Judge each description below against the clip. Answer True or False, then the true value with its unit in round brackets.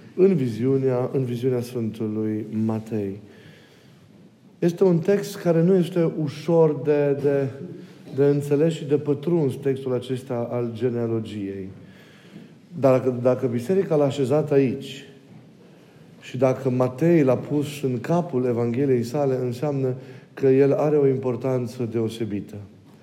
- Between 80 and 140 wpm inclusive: True (120 wpm)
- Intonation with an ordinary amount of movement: True (3.6 semitones)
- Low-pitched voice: True (130 Hz)